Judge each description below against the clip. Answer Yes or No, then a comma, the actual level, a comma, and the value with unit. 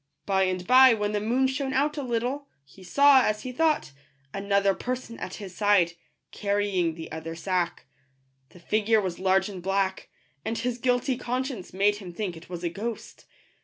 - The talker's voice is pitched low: No, high, 205 Hz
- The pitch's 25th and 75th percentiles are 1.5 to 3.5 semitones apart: No, average, 5.0 semitones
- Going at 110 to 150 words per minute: No, average, 180 wpm